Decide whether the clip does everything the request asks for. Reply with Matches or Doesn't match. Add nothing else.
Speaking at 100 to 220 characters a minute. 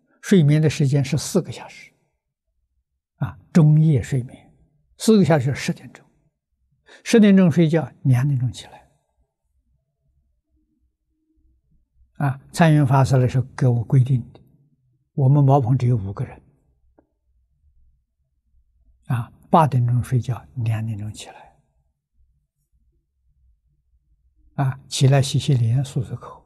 Matches